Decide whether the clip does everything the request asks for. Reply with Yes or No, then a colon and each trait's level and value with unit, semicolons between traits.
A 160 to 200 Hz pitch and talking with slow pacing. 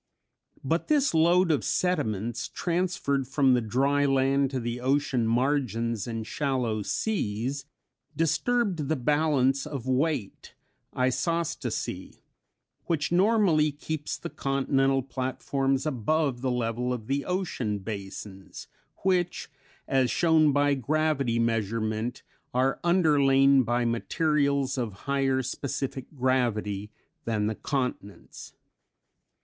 No: low, 135 Hz; slow, 110 wpm